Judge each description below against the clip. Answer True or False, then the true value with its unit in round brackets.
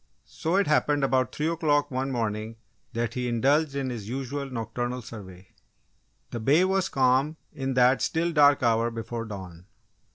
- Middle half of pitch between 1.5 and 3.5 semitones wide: False (4.1 semitones)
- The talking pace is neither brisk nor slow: True (160 wpm)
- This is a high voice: False (130 Hz)